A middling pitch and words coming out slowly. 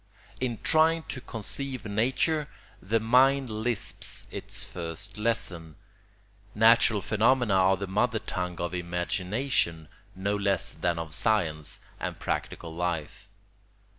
No: low, 105 Hz; slow, 115 wpm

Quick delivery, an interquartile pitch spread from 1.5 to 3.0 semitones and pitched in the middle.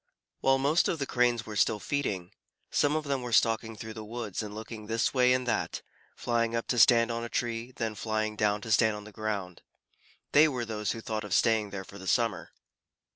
No: fast, 225 wpm; narrow, 2.4 semitones; low, 115 Hz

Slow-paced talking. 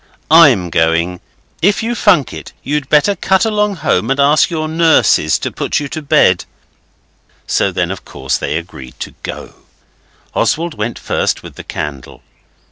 No: average, 160 wpm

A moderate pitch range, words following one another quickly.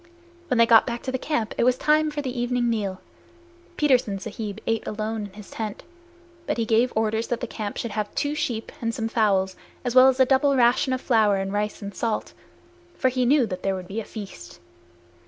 Yes: average, 3.3 semitones; fast, 215 wpm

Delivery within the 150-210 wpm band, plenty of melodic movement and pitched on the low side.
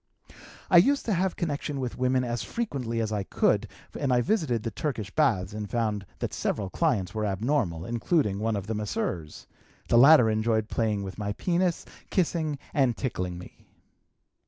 Yes: average, 175 wpm; wide, 6.0 semitones; low, 115 Hz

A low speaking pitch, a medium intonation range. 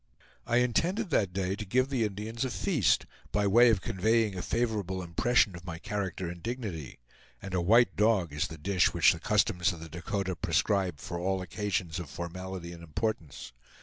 Yes: very low, 95 Hz; average, 4.4 semitones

